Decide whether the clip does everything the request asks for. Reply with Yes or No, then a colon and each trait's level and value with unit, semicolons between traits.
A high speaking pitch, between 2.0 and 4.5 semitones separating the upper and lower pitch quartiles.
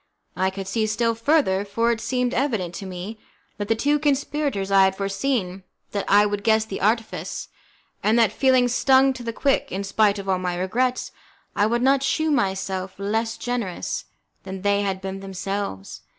Yes: high, 210 Hz; average, 4.2 semitones